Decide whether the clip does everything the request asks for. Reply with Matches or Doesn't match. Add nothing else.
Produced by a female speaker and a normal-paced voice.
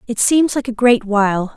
Doesn't match